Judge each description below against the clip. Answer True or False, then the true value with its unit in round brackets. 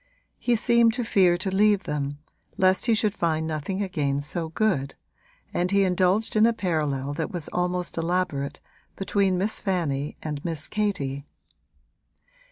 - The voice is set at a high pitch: False (180 Hz)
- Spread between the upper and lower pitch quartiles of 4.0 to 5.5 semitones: True (5.1 semitones)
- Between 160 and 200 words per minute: False (150 wpm)